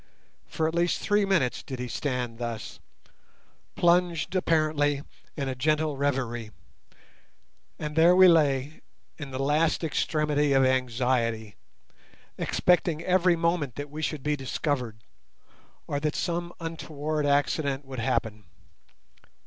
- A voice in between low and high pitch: Yes, medium, 145 Hz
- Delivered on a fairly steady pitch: No, average, 3.9 semitones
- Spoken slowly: Yes, slow, 125 wpm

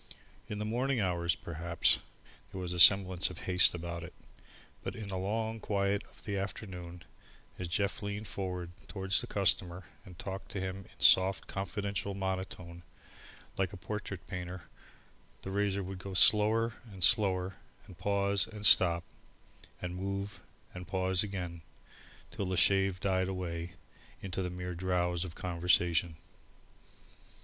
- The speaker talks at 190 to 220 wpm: No, average, 145 wpm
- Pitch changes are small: Yes, narrow, 2.0 semitones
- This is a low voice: Yes, very low, 95 Hz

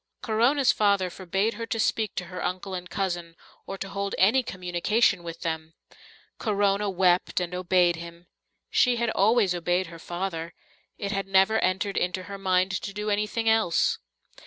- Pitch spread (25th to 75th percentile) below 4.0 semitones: Yes, average, 2.8 semitones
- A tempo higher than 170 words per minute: No, average, 165 wpm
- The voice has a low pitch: No, high, 190 Hz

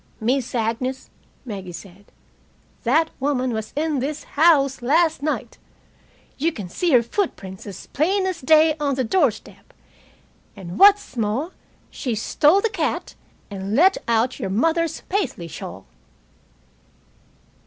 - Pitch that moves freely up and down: Yes, wide, 6.6 semitones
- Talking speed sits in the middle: No, slow, 130 wpm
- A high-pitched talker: Yes, very high, 265 Hz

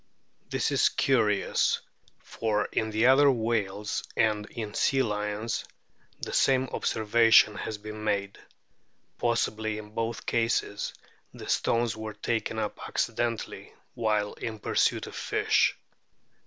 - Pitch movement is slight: Yes, narrow, 1.8 semitones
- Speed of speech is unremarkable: No, slow, 115 wpm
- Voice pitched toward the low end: Yes, low, 110 Hz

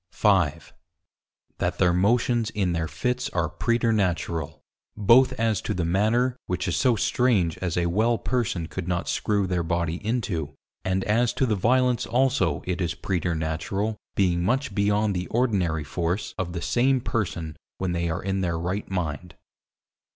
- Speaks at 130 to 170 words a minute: Yes, average, 160 wpm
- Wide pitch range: No, average, 4.8 semitones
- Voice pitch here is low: Yes, very low, 95 Hz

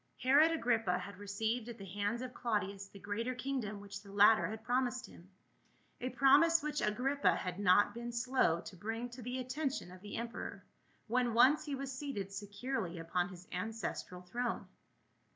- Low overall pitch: No, high, 225 Hz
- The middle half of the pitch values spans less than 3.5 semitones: No, average, 4.3 semitones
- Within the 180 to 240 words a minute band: No, average, 170 wpm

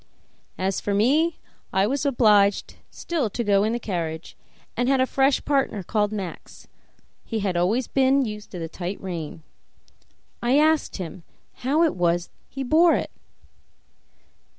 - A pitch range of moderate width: No, wide, 6.2 semitones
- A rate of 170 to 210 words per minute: No, average, 150 wpm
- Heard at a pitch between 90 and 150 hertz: No, high, 215 Hz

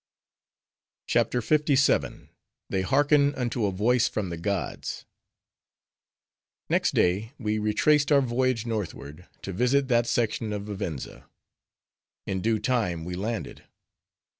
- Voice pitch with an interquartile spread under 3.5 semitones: No, average, 4.7 semitones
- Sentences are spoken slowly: Yes, slow, 115 wpm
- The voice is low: Yes, low, 110 Hz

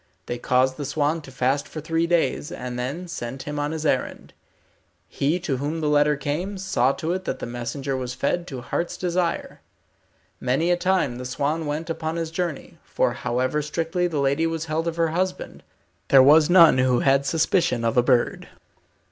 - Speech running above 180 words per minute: Yes, average, 190 wpm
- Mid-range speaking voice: Yes, medium, 150 Hz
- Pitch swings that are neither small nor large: Yes, average, 4.1 semitones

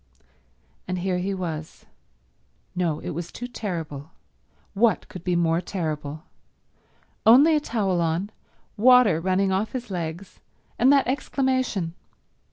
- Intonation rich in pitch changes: Yes, wide, 5.8 semitones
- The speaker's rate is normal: No, slow, 125 wpm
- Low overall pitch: No, medium, 185 Hz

